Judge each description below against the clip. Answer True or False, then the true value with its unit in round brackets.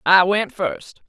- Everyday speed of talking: True (165 wpm)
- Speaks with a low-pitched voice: False (190 Hz)